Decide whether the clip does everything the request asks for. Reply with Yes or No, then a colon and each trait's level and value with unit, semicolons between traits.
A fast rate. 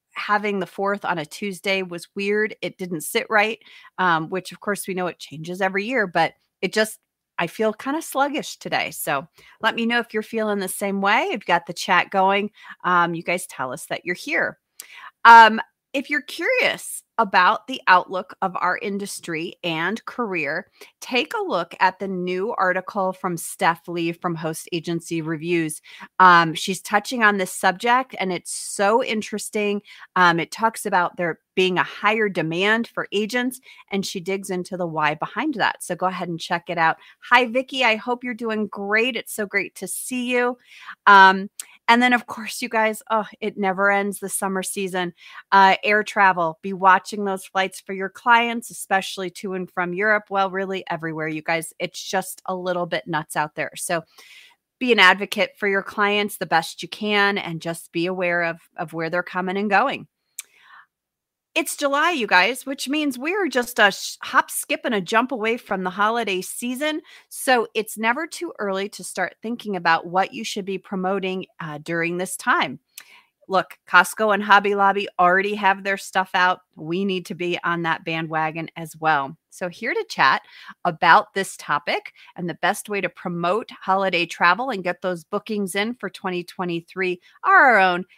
No: average, 185 wpm